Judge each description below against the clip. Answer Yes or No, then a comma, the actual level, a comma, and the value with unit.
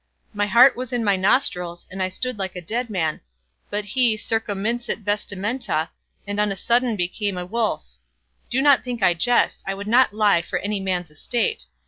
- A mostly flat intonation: No, average, 4.2 semitones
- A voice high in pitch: Yes, high, 210 Hz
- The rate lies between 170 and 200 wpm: Yes, average, 185 wpm